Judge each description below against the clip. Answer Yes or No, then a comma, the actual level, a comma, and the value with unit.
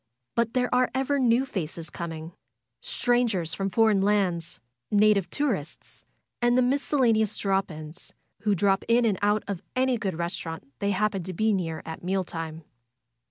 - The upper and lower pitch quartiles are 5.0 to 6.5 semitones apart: Yes, average, 5.3 semitones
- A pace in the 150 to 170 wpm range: Yes, average, 160 wpm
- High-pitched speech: Yes, high, 200 Hz